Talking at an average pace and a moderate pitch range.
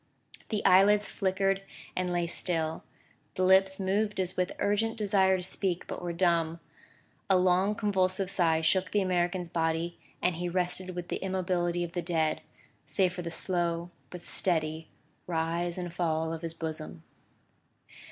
No: average, 160 wpm; narrow, 2.0 semitones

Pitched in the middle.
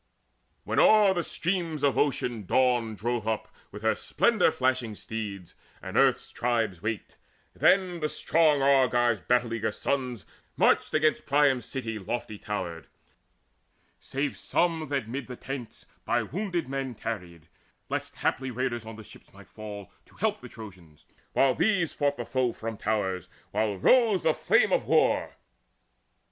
No: low, 125 Hz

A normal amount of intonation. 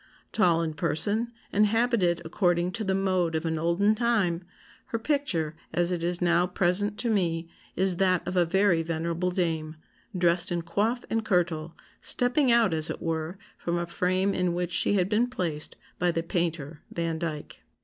Yes: average, 3.2 semitones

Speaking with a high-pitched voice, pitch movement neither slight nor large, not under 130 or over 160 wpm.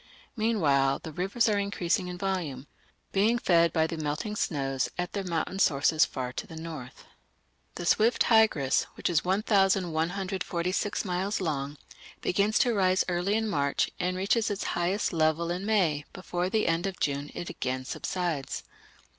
No: medium, 180 Hz; average, 4.1 semitones; average, 155 wpm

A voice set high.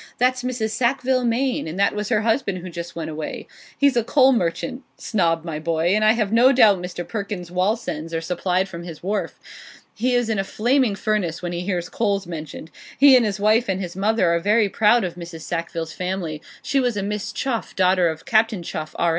Yes: high, 200 Hz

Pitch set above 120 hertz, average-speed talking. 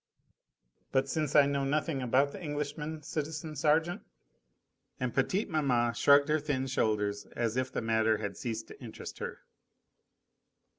Yes: medium, 140 Hz; average, 150 wpm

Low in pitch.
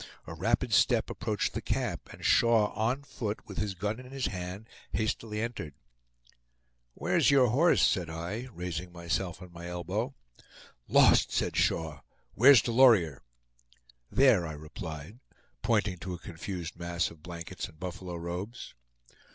Yes: very low, 95 Hz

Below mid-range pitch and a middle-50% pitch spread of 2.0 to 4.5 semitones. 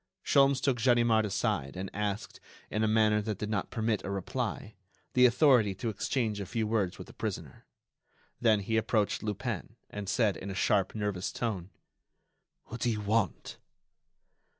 Yes: low, 110 Hz; narrow, 2.5 semitones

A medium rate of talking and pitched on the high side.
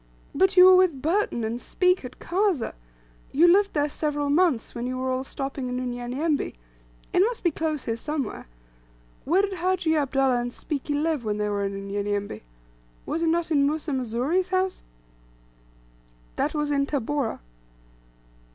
Yes: average, 160 wpm; very high, 290 Hz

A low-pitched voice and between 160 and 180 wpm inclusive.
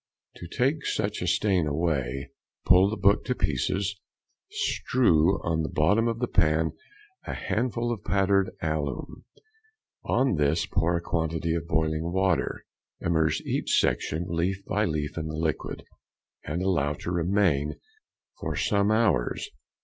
No: very low, 85 Hz; average, 140 wpm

